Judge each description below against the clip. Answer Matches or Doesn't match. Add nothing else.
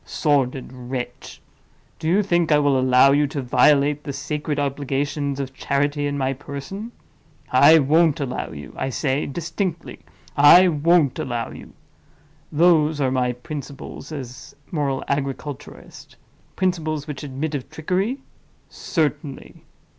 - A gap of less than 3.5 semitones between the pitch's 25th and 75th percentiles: Matches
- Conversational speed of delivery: Doesn't match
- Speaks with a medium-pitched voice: Matches